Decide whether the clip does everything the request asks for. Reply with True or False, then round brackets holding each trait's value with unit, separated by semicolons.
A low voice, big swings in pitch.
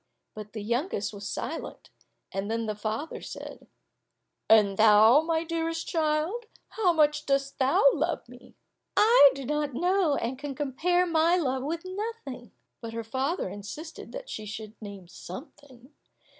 False (275 Hz; 6.8 semitones)